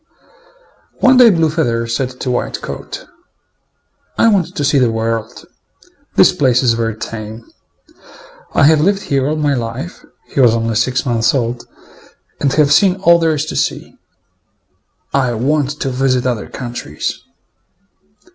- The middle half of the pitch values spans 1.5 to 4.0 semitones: No, average, 4.7 semitones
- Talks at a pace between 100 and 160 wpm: Yes, average, 150 wpm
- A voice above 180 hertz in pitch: No, low, 130 Hz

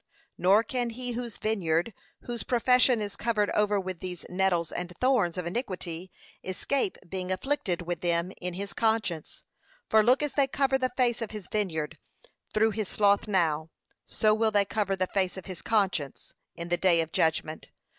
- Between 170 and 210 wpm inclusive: Yes, average, 175 wpm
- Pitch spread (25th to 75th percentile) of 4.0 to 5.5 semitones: Yes, average, 4.3 semitones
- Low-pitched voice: No, high, 200 Hz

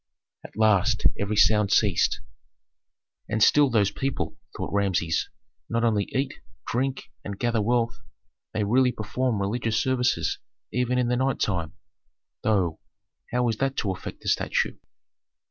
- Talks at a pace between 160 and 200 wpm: No, average, 140 wpm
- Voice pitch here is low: Yes, low, 110 Hz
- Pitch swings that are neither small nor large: Yes, average, 3.4 semitones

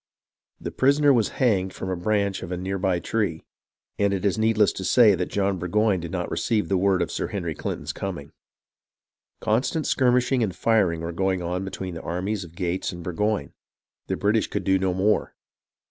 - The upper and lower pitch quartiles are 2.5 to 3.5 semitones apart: Yes, average, 3.1 semitones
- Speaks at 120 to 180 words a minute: No, average, 190 wpm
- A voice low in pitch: Yes, very low, 95 Hz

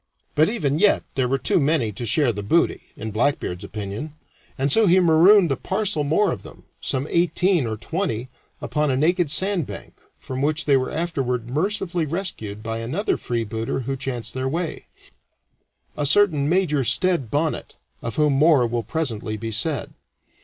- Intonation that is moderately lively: No, wide, 5.9 semitones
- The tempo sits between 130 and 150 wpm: No, average, 170 wpm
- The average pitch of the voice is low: No, medium, 145 Hz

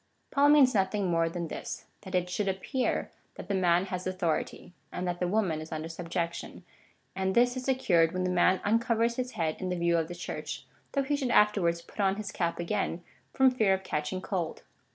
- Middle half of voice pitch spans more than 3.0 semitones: Yes, average, 3.9 semitones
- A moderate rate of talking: No, fast, 215 wpm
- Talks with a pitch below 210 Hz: Yes, medium, 185 Hz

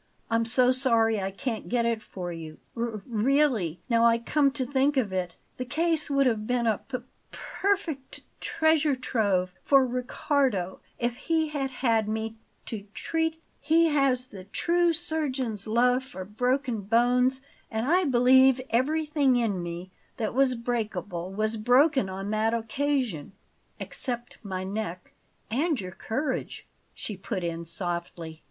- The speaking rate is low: No, average, 150 wpm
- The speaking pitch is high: Yes, high, 240 Hz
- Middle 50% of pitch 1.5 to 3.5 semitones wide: No, average, 4.7 semitones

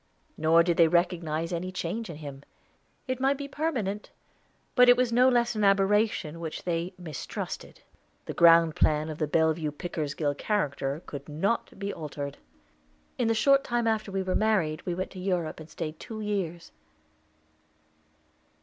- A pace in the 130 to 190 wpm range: Yes, average, 160 wpm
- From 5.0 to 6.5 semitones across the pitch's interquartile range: Yes, wide, 5.4 semitones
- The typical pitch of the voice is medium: Yes, medium, 175 Hz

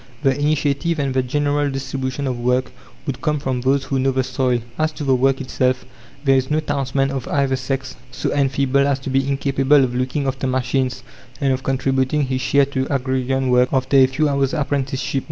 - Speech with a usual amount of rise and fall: No, narrow, 1.3 semitones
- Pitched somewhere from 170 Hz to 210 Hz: No, low, 135 Hz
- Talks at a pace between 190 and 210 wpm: Yes, average, 200 wpm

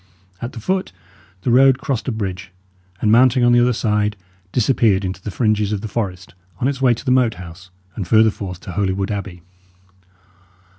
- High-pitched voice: No, low, 110 Hz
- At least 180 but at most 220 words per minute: Yes, average, 190 wpm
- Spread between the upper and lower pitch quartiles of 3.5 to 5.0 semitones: Yes, average, 4.2 semitones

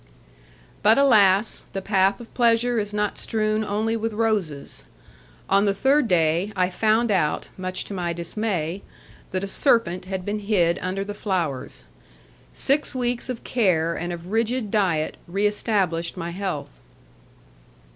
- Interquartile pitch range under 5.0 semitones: Yes, average, 3.7 semitones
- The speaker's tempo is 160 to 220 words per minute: No, average, 145 wpm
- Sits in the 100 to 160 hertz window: No, high, 200 Hz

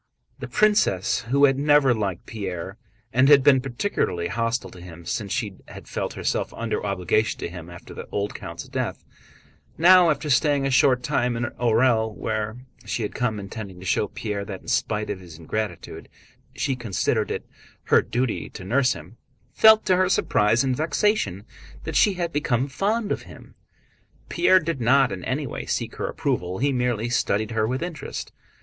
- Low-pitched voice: Yes, low, 120 Hz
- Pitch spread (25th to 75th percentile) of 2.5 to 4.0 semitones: No, wide, 5.4 semitones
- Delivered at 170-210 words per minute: Yes, average, 175 wpm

